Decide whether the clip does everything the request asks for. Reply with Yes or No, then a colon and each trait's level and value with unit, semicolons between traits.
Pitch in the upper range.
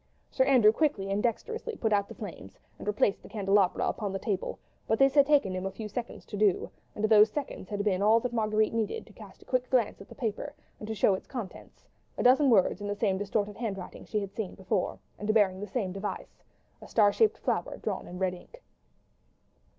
Yes: high, 210 Hz